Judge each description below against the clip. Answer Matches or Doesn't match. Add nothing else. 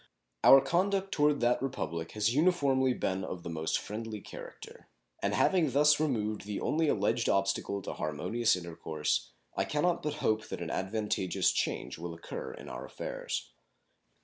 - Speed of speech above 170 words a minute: Doesn't match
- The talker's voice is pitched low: Matches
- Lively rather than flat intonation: Matches